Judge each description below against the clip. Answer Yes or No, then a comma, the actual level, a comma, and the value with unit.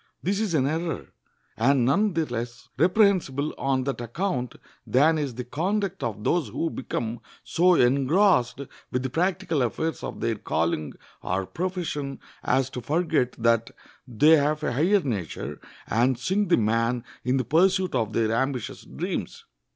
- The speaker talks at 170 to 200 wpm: No, average, 155 wpm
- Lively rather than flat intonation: Yes, wide, 6.1 semitones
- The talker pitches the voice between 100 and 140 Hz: Yes, low, 135 Hz